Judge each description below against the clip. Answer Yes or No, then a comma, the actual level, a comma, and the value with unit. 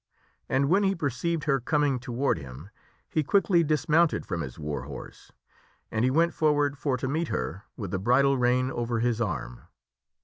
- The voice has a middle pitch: No, low, 130 Hz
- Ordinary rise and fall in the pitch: No, wide, 6.7 semitones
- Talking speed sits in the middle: Yes, average, 190 wpm